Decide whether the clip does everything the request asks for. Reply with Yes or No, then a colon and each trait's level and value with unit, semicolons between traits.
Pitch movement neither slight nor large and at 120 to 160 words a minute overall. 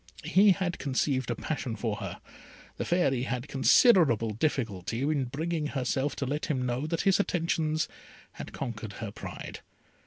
Yes: average, 4.8 semitones; average, 155 wpm